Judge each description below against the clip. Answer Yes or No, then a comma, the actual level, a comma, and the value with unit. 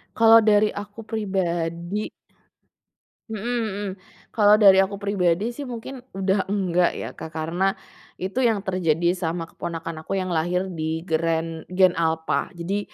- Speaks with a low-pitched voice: No, high, 190 Hz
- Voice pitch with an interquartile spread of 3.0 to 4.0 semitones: Yes, average, 3.7 semitones